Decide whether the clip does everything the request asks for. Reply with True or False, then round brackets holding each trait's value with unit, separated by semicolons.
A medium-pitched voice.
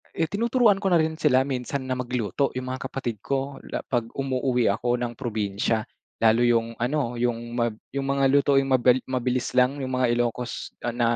False (125 Hz)